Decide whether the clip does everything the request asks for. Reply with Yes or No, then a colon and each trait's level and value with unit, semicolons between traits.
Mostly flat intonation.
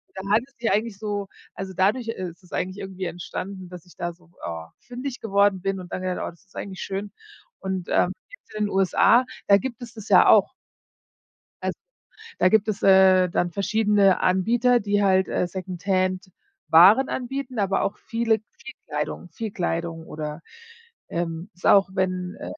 No: average, 3.1 semitones